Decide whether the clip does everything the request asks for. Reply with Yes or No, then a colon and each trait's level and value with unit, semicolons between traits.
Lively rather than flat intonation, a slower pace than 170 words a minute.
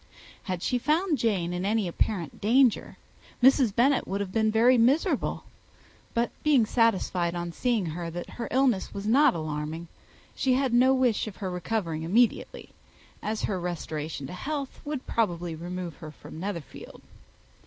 Yes: wide, 6.2 semitones; average, 155 wpm